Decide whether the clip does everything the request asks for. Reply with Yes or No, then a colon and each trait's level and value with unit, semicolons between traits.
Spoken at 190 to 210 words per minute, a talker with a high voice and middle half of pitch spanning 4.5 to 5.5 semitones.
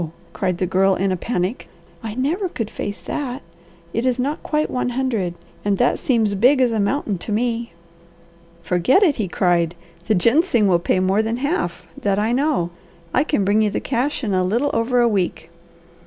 Yes: average, 195 wpm; high, 225 Hz; average, 5.0 semitones